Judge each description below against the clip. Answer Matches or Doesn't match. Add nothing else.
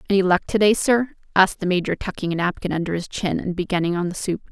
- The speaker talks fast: Matches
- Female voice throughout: Matches